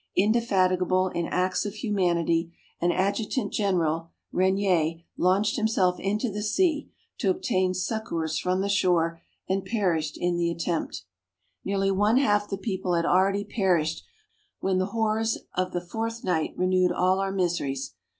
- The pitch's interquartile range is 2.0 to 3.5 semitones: Yes, average, 2.9 semitones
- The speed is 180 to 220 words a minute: No, average, 145 wpm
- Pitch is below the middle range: No, medium, 185 Hz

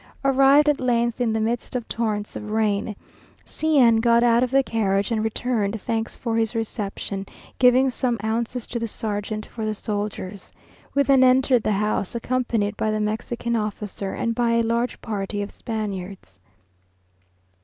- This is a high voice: Yes, high, 225 Hz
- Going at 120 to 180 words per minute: Yes, average, 165 wpm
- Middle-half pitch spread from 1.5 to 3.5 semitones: Yes, narrow, 2.5 semitones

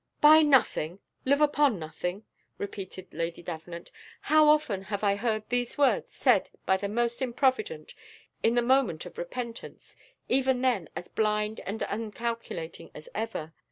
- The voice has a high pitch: Yes, high, 225 Hz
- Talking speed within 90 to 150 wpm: Yes, average, 145 wpm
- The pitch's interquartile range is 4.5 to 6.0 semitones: Yes, wide, 5.6 semitones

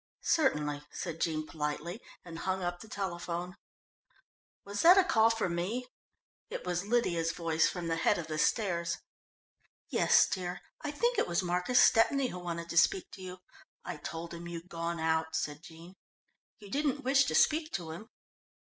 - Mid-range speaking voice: Yes, medium, 175 Hz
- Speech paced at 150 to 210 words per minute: Yes, average, 175 wpm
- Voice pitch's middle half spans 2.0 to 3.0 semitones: No, average, 4.7 semitones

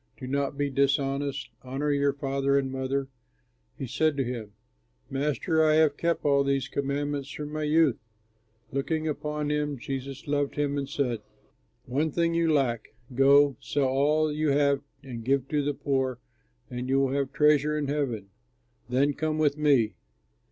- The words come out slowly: No, average, 165 wpm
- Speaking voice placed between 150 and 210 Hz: No, medium, 140 Hz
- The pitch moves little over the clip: Yes, narrow, 1.8 semitones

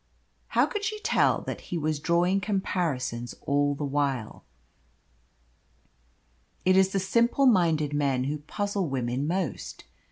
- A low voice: No, medium, 160 Hz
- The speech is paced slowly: Yes, slow, 130 wpm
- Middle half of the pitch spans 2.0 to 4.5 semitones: No, average, 5.3 semitones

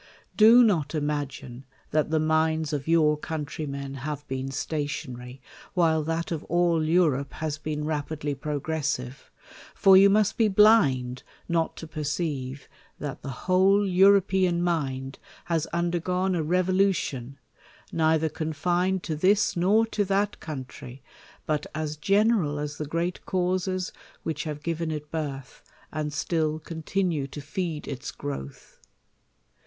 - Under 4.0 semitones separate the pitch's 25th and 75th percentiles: Yes, average, 3.6 semitones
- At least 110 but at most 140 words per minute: Yes, slow, 135 wpm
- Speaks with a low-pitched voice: No, medium, 155 Hz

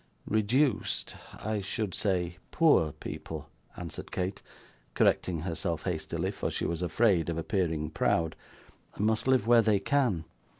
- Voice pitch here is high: No, very low, 95 Hz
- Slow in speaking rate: Yes, slow, 130 wpm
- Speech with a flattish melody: No, average, 4.7 semitones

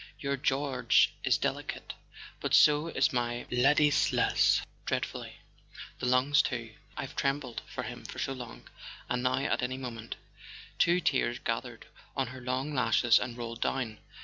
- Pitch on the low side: Yes, low, 125 Hz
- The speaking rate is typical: Yes, average, 150 wpm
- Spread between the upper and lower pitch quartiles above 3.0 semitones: No, narrow, 2.4 semitones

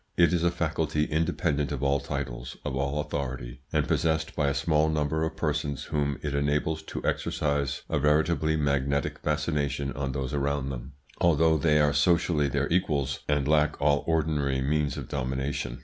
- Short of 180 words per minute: Yes, average, 170 wpm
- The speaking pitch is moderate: No, very low, 75 Hz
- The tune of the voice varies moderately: No, narrow, 1.9 semitones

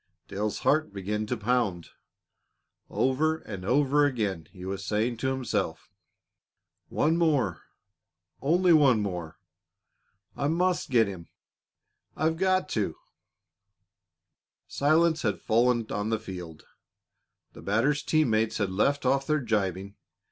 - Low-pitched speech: Yes, low, 115 Hz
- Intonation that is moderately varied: No, wide, 6.6 semitones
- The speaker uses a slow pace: Yes, slow, 120 wpm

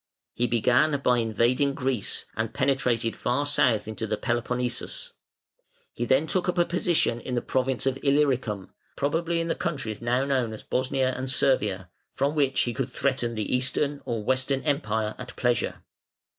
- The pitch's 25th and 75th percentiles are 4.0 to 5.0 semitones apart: No, average, 3.0 semitones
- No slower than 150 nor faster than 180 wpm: Yes, average, 165 wpm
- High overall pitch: No, low, 130 Hz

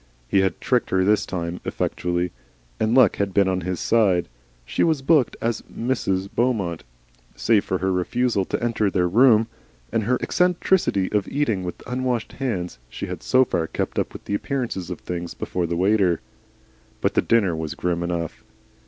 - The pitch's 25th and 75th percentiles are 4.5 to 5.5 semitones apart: Yes, average, 5.1 semitones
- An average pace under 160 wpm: No, average, 175 wpm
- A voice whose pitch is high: No, low, 100 Hz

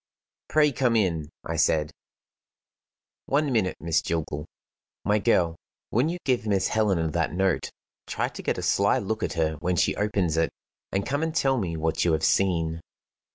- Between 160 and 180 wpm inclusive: Yes, average, 175 wpm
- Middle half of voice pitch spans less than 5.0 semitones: No, average, 5.3 semitones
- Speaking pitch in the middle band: No, very low, 95 Hz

